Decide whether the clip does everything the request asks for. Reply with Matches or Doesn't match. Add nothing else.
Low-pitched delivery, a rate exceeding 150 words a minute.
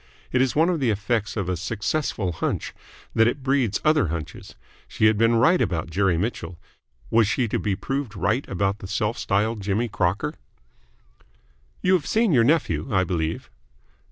Matches